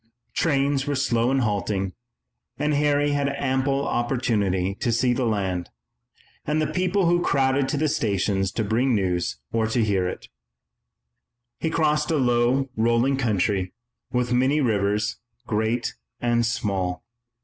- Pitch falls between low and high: No, low, 120 Hz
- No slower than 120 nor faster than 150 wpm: Yes, average, 140 wpm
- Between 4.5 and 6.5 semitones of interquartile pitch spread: Yes, average, 5.0 semitones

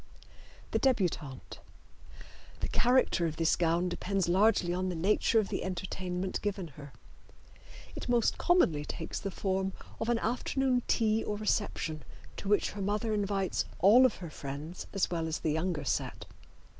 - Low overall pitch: No, high, 190 Hz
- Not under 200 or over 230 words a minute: No, average, 155 wpm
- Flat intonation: No, average, 4.2 semitones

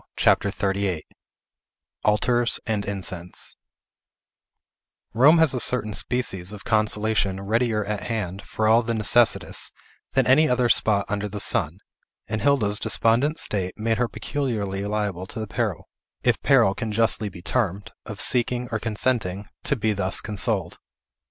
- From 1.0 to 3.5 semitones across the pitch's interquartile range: Yes, average, 3.2 semitones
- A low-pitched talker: Yes, low, 105 Hz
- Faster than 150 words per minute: No, average, 145 wpm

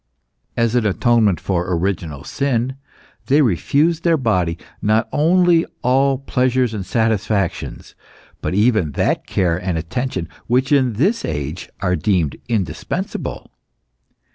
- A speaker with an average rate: No, slow, 120 wpm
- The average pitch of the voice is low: Yes, low, 110 Hz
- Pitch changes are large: Yes, wide, 6.4 semitones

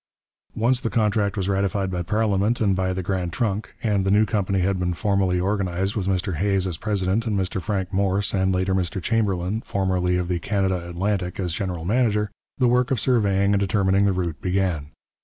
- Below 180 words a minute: No, average, 195 wpm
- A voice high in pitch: No, very low, 95 Hz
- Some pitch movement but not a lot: No, narrow, 2.1 semitones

